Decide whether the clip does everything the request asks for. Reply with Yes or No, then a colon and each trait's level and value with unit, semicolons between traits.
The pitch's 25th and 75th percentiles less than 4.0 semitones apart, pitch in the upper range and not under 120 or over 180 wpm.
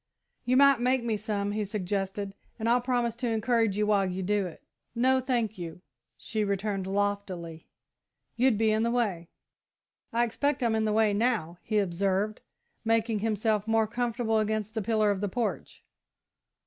Yes: narrow, 2.6 semitones; high, 215 Hz; average, 170 wpm